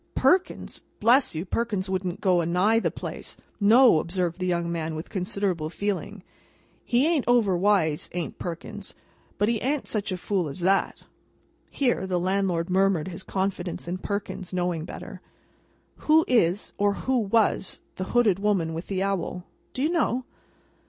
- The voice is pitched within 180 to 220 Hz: Yes, high, 190 Hz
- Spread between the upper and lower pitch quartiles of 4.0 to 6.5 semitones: No, average, 3.4 semitones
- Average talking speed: Yes, average, 150 wpm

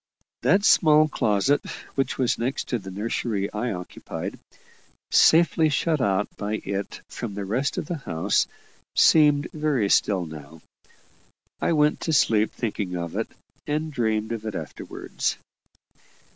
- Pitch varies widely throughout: Yes, wide, 6.8 semitones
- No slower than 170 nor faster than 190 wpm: No, average, 140 wpm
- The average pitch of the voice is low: Yes, low, 115 Hz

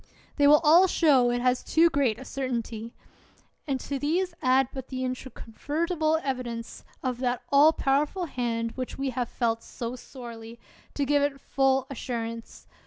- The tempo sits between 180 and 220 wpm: No, average, 160 wpm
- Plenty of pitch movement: No, average, 3.0 semitones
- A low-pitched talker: No, very high, 260 Hz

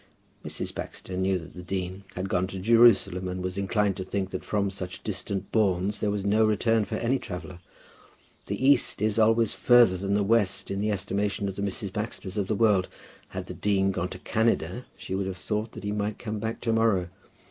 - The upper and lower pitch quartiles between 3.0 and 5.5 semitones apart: No, narrow, 2.5 semitones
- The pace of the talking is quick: Yes, fast, 210 wpm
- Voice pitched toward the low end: Yes, low, 100 Hz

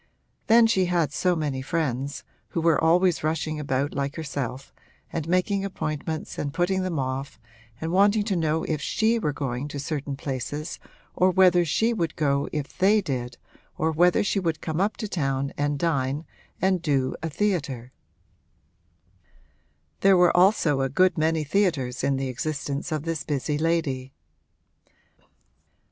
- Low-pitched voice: No, medium, 155 Hz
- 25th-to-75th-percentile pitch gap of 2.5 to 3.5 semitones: No, average, 4.3 semitones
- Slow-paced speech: No, average, 155 wpm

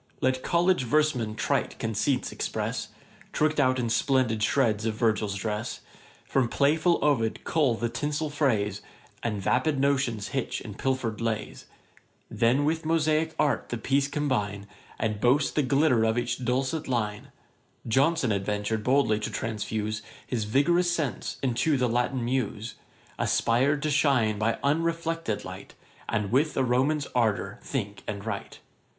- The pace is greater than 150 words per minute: No, average, 145 wpm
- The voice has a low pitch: Yes, low, 125 Hz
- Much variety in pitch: No, average, 4.8 semitones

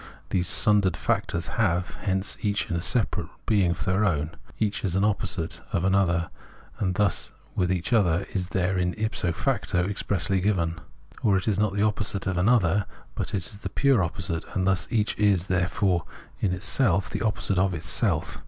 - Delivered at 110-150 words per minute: No, average, 185 wpm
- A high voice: No, very low, 95 Hz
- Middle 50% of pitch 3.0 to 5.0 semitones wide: No, narrow, 2.6 semitones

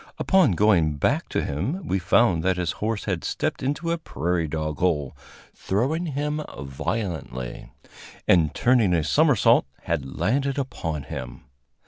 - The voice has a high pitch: No, very low, 90 Hz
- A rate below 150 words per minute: Yes, average, 140 wpm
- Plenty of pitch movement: Yes, wide, 8.8 semitones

